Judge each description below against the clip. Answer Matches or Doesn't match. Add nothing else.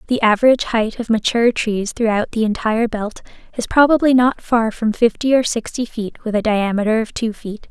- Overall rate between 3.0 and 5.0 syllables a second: Doesn't match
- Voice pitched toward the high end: Matches